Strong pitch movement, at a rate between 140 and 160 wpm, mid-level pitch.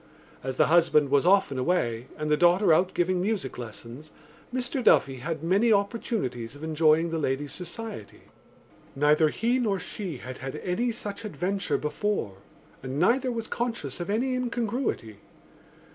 Yes: wide, 7.2 semitones; average, 150 wpm; medium, 175 Hz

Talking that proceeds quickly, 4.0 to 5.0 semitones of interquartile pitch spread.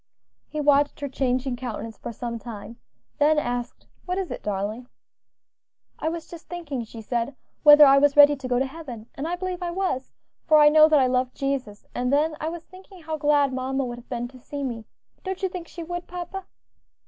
Yes: fast, 210 wpm; average, 4.6 semitones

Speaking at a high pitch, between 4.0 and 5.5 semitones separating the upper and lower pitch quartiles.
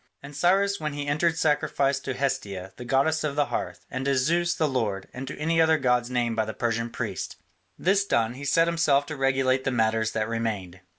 No: low, 135 Hz; average, 4.7 semitones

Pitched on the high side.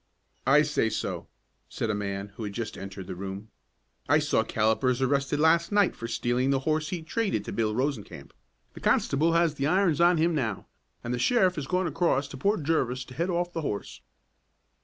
No: medium, 140 Hz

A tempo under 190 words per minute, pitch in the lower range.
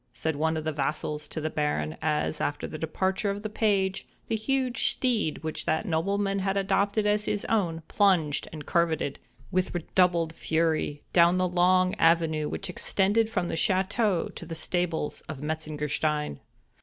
No: average, 165 wpm; medium, 170 Hz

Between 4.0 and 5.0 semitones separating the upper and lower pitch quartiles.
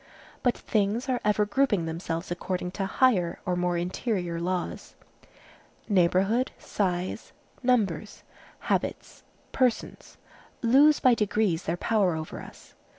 Yes: average, 4.6 semitones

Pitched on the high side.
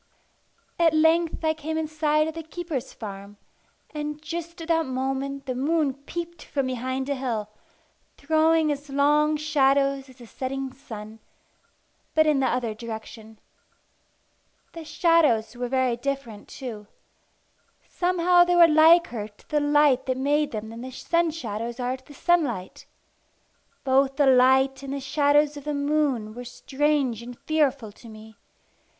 Yes: very high, 275 Hz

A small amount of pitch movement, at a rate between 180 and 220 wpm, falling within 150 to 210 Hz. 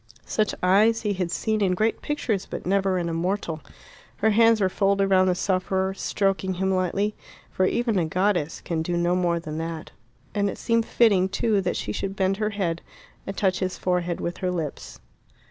Yes: narrow, 2.3 semitones; average, 195 wpm; high, 190 Hz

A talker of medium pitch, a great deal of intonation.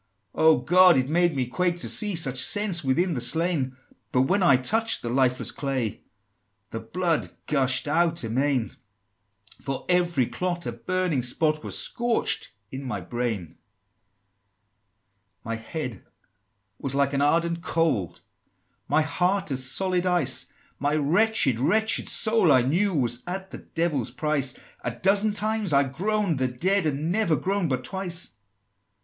Yes: medium, 155 Hz; wide, 5.8 semitones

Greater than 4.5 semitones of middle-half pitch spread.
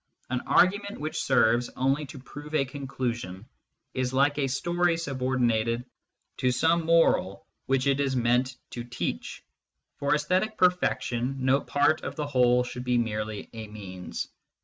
No: average, 3.5 semitones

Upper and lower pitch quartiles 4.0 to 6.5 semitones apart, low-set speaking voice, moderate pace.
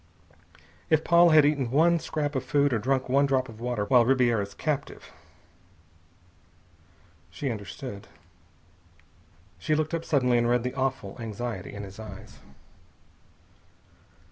No: average, 4.3 semitones; low, 130 Hz; slow, 130 wpm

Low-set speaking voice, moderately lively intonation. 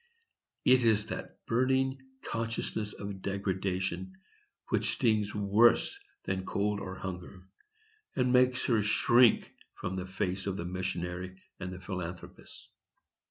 Yes: low, 100 Hz; average, 3.6 semitones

